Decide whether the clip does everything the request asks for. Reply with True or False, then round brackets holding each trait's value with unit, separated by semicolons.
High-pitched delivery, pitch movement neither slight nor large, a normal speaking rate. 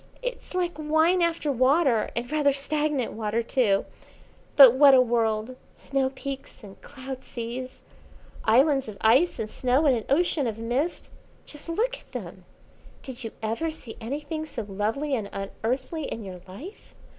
True (265 Hz; 4.9 semitones; 155 wpm)